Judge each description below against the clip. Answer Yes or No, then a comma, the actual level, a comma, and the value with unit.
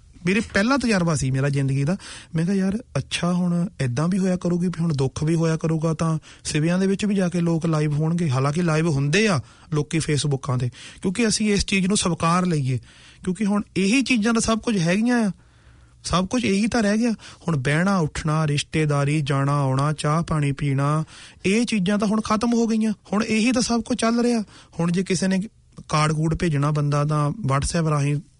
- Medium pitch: Yes, medium, 170 Hz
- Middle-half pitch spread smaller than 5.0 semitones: No, wide, 5.4 semitones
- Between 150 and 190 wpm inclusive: No, average, 200 wpm